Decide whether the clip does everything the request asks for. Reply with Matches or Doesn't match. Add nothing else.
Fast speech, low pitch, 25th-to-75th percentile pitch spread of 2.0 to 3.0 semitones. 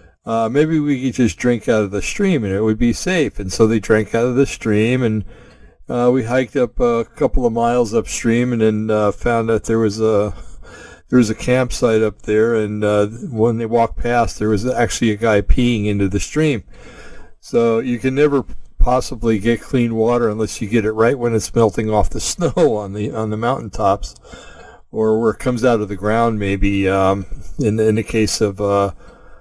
Matches